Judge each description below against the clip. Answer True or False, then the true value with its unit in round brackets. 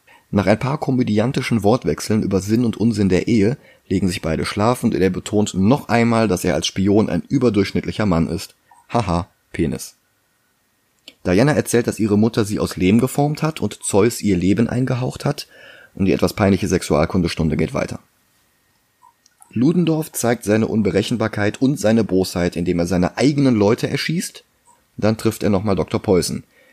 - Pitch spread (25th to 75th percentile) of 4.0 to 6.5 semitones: True (4.7 semitones)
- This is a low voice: True (105 Hz)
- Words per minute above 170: False (160 wpm)